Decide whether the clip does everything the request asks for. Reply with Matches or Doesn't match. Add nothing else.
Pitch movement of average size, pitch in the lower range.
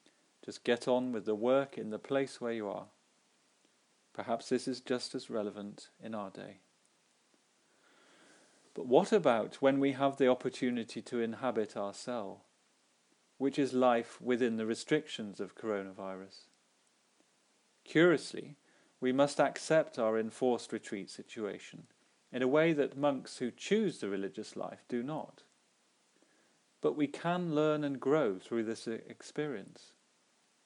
Matches